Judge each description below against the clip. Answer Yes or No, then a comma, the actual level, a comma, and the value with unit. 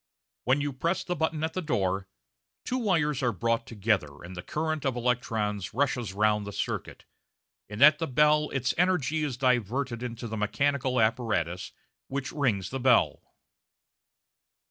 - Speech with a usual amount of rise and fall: No, wide, 5.7 semitones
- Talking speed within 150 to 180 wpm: Yes, average, 155 wpm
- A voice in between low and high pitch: No, low, 125 Hz